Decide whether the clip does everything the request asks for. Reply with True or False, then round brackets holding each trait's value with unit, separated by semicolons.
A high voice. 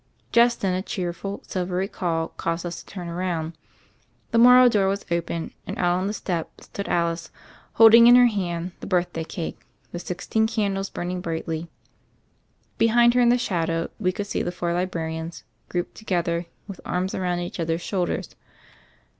False (180 Hz)